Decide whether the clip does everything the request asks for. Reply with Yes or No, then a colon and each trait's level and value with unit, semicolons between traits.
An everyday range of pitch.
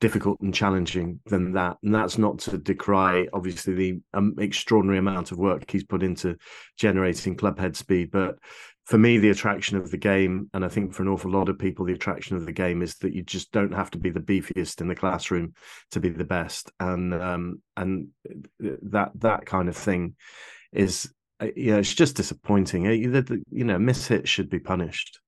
No: narrow, 1.9 semitones